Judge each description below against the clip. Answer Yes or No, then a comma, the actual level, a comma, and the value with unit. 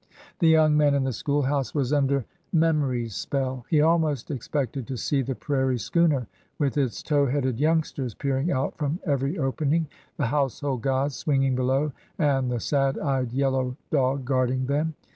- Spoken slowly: No, average, 170 wpm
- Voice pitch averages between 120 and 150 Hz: Yes, medium, 140 Hz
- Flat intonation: Yes, narrow, 2.3 semitones